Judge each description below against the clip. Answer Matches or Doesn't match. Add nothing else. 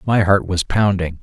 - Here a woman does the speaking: Doesn't match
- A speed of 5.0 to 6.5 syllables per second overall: Doesn't match